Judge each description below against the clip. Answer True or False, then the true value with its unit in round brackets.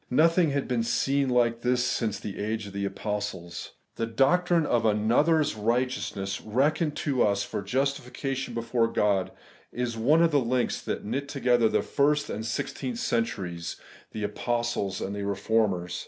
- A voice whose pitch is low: True (115 Hz)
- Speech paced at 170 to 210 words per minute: False (160 wpm)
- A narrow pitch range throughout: False (4.6 semitones)